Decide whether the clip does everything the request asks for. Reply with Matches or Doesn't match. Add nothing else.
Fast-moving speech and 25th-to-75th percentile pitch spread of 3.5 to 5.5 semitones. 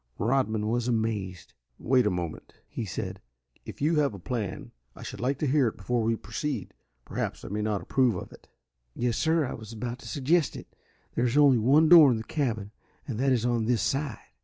Matches